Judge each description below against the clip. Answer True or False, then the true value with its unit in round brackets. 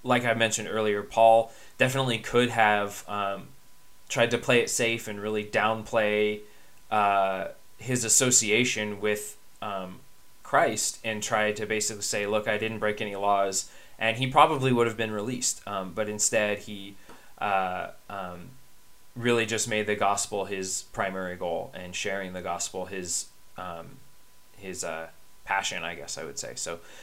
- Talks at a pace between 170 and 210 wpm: False (155 wpm)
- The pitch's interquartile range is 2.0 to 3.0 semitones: True (2.5 semitones)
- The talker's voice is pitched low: True (105 Hz)